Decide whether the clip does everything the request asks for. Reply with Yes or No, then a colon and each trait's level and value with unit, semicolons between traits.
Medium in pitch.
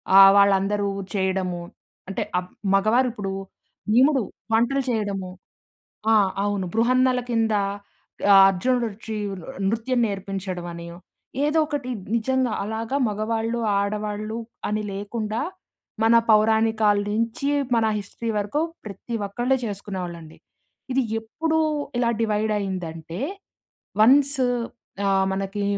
No: high, 215 Hz